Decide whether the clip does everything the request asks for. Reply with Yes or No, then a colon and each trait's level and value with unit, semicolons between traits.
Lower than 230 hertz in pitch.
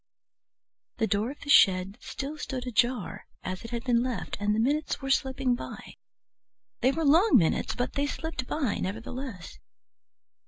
No: very high, 250 Hz